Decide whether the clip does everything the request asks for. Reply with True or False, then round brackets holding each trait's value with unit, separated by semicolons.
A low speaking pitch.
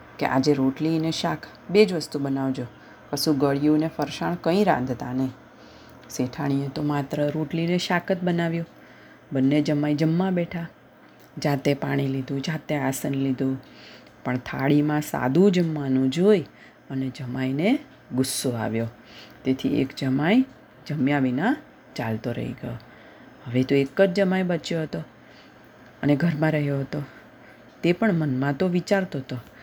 False (145 Hz)